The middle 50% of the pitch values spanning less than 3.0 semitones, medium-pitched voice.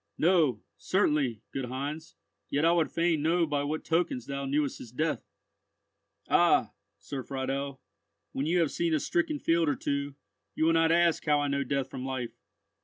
No: average, 3.3 semitones; medium, 145 Hz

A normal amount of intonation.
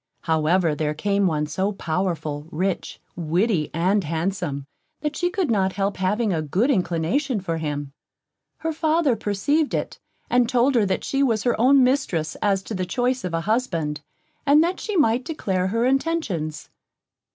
No: wide, 7.4 semitones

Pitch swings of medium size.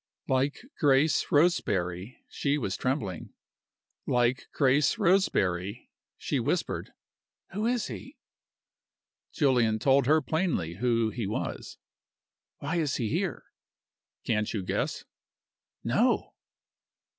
No: wide, 6.1 semitones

